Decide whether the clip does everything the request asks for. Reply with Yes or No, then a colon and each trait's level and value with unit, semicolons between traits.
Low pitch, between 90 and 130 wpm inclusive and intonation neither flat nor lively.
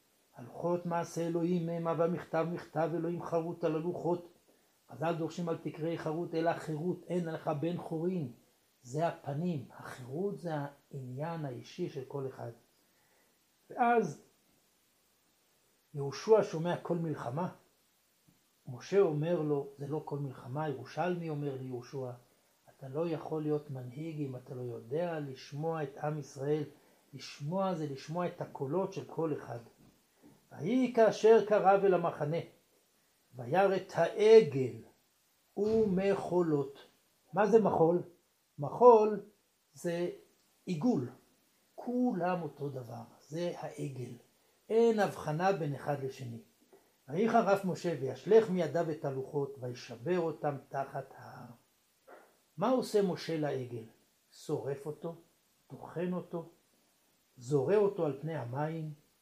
No: medium, 160 Hz; average, 120 wpm; average, 3.8 semitones